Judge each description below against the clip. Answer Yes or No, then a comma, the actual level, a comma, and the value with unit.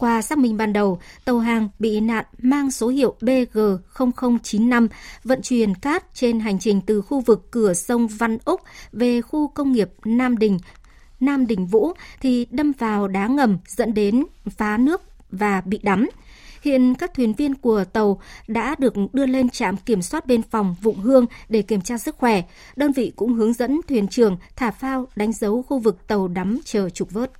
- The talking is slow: No, average, 190 wpm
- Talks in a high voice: Yes, high, 230 Hz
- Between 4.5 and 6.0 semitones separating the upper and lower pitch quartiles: No, average, 3.4 semitones